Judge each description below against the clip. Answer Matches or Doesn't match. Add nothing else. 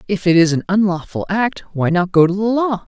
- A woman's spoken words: Matches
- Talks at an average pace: Doesn't match